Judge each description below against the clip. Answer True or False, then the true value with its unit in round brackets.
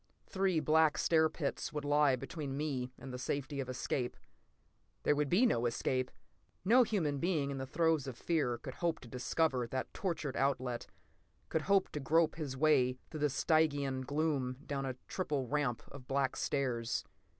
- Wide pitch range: False (3.5 semitones)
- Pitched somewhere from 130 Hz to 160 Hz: True (140 Hz)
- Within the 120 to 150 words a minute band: False (170 wpm)